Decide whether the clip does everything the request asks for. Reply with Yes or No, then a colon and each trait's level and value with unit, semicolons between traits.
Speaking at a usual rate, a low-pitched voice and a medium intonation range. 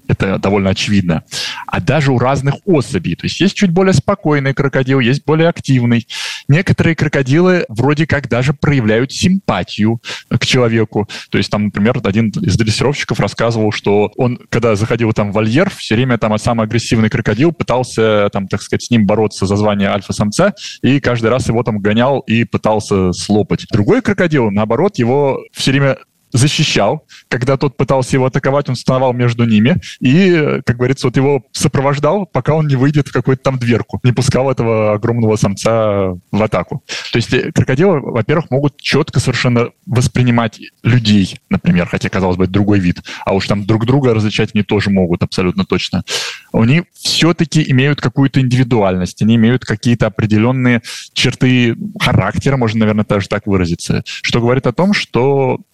No: fast, 165 wpm; low, 120 Hz; average, 4.5 semitones